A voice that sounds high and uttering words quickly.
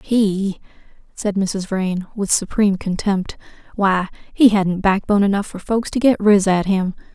No: high, 200 Hz; average, 160 wpm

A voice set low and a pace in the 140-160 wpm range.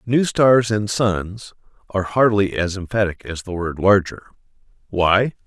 Yes: low, 100 Hz; average, 145 wpm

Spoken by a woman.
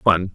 No: male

